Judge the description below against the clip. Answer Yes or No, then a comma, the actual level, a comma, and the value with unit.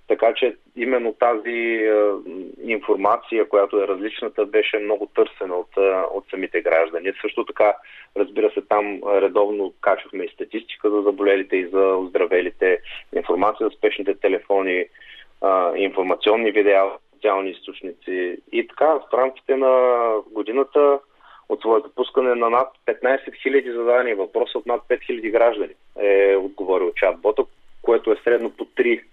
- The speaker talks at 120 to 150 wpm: Yes, average, 140 wpm